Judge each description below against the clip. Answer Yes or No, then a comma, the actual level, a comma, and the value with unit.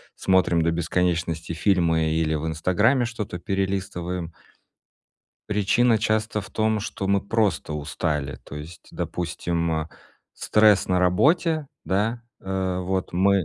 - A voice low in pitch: Yes, very low, 95 Hz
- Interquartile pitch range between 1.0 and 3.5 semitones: No, average, 3.9 semitones